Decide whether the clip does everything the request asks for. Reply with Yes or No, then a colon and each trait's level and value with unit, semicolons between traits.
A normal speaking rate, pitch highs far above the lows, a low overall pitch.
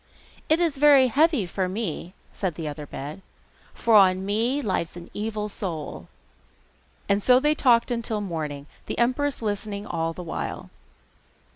No: average, 160 wpm; wide, 6.1 semitones; high, 205 Hz